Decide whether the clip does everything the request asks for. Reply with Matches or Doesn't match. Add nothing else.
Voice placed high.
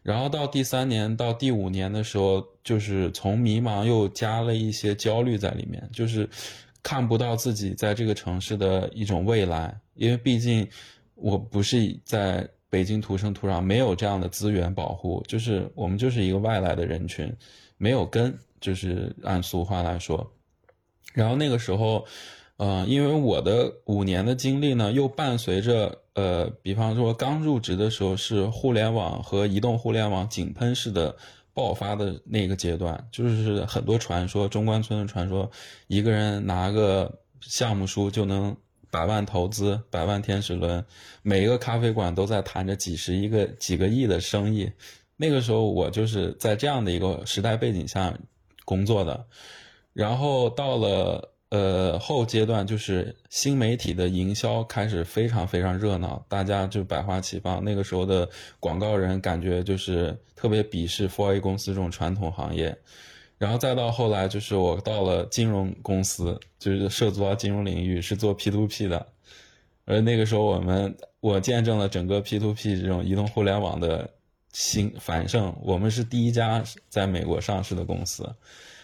Doesn't match